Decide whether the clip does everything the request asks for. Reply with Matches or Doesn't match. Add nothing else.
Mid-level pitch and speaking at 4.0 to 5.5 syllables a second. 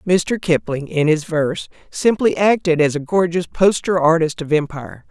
Matches